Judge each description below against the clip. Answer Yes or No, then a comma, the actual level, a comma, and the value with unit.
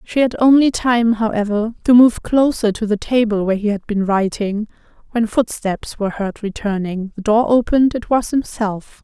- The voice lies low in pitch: No, high, 220 Hz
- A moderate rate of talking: Yes, average, 180 wpm